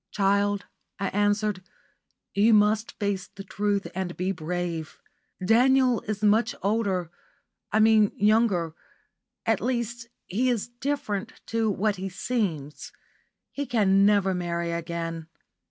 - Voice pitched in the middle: No, high, 205 Hz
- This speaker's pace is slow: Yes, slow, 120 wpm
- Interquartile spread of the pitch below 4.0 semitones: Yes, average, 3.3 semitones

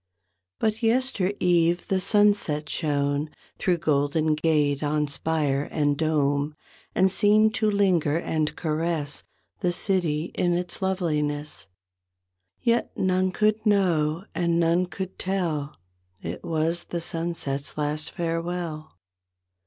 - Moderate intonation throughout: Yes, average, 3.8 semitones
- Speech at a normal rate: No, slow, 115 wpm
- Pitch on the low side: No, medium, 165 Hz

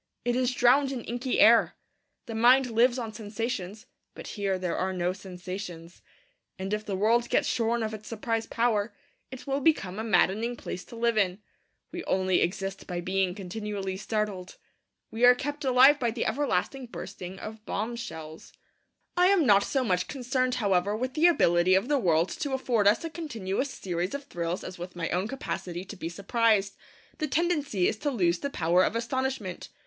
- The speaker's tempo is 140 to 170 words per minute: No, average, 185 wpm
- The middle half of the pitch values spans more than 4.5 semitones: Yes, average, 5.1 semitones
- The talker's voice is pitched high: Yes, high, 215 Hz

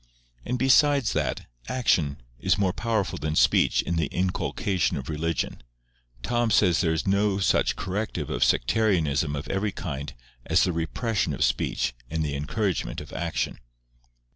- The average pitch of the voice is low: Yes, very low, 90 Hz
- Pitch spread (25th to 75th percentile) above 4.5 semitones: Yes, wide, 5.5 semitones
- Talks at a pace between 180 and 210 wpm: No, average, 150 wpm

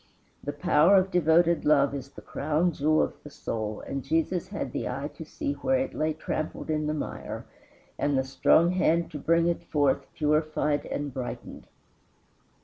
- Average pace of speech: Yes, average, 175 wpm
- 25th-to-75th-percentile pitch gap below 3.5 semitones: Yes, average, 2.8 semitones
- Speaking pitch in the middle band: Yes, medium, 155 Hz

